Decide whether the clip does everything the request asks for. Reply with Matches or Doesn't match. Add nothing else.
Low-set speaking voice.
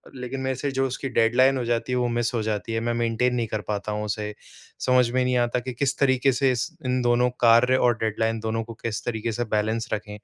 Matches